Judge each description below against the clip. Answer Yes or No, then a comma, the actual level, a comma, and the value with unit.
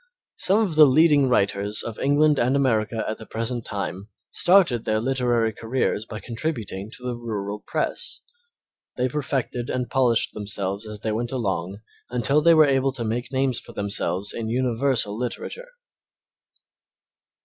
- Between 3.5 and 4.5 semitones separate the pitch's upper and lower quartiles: Yes, average, 3.8 semitones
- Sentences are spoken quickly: No, average, 150 wpm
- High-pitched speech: No, low, 120 Hz